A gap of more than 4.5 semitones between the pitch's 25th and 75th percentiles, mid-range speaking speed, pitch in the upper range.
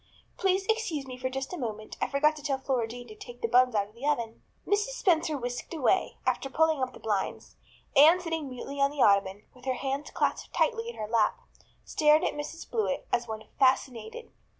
No: average, 4.9 semitones; fast, 210 wpm; very high, 270 Hz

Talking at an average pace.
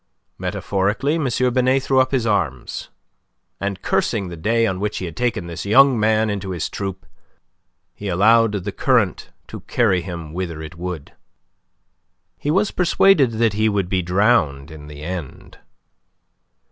Yes: average, 155 wpm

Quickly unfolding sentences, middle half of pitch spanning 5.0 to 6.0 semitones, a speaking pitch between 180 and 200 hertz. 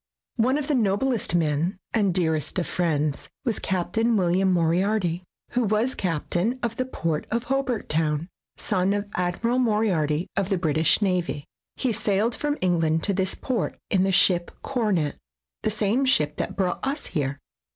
No: average, 165 wpm; average, 5.3 semitones; high, 190 Hz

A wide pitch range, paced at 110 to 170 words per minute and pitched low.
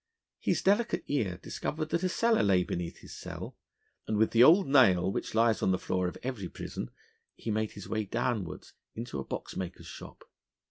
No: wide, 6.9 semitones; average, 185 wpm; low, 110 Hz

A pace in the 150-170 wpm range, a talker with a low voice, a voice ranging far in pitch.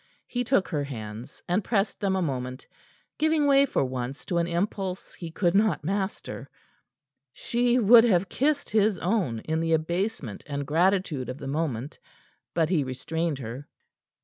No: average, 160 wpm; medium, 170 Hz; wide, 6.5 semitones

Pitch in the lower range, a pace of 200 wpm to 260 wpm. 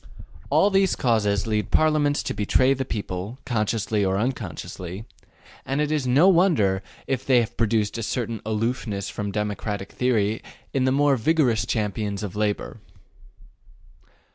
No: low, 115 Hz; average, 140 wpm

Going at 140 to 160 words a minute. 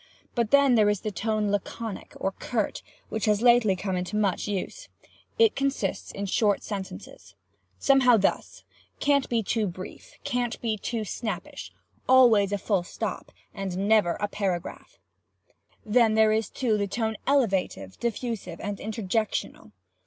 Yes: average, 145 wpm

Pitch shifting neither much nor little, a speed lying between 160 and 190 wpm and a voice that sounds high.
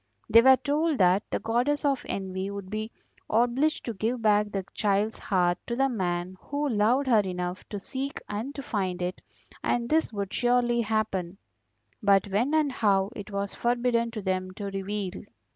Yes: average, 4.0 semitones; average, 175 wpm; high, 215 Hz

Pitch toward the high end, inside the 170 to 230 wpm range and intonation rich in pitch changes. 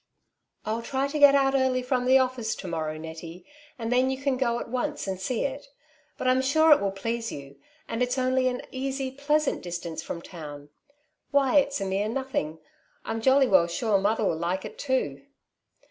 Yes: high, 245 Hz; average, 200 wpm; wide, 5.9 semitones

